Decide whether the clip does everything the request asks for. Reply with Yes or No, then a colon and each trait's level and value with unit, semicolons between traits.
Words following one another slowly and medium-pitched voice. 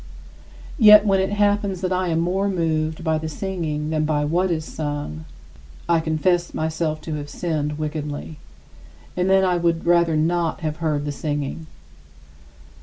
No: average, 160 wpm; medium, 160 Hz